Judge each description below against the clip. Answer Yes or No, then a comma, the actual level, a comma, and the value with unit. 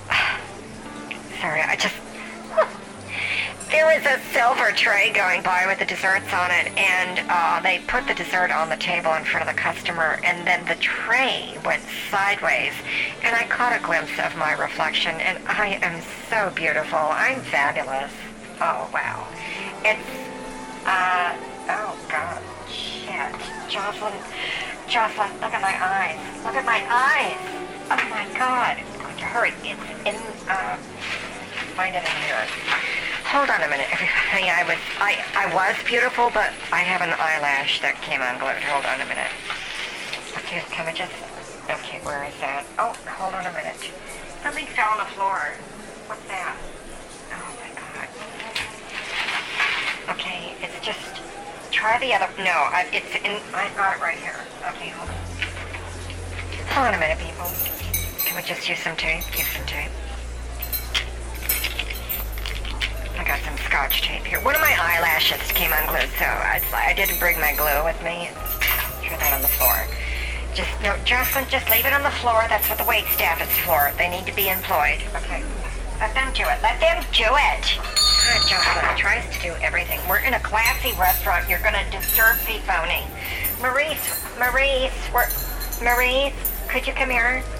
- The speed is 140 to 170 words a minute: Yes, average, 165 wpm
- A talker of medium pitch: Yes, medium, 175 Hz